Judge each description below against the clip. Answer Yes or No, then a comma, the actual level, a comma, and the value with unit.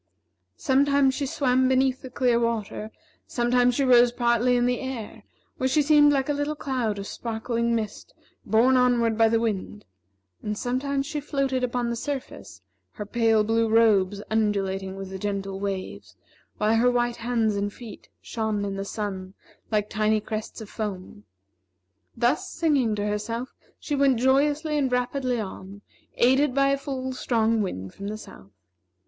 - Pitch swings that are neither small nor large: Yes, average, 3.7 semitones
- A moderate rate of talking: Yes, average, 165 wpm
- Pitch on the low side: No, high, 235 Hz